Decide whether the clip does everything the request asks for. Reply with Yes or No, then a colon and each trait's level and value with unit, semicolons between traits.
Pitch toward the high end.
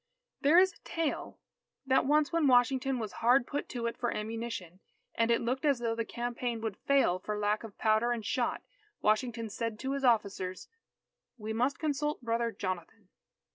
Yes: high, 235 Hz